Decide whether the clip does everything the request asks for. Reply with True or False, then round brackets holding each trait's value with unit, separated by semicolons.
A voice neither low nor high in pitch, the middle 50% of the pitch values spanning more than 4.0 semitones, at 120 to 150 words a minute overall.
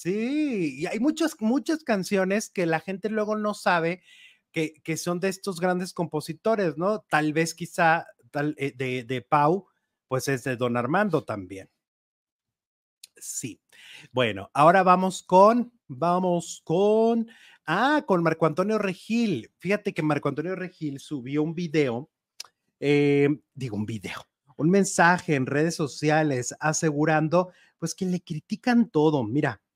True (170 Hz; 5.1 semitones; 140 wpm)